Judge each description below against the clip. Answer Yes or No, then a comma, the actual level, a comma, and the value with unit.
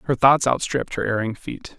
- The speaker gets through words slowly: No, average, 200 wpm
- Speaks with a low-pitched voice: Yes, low, 125 Hz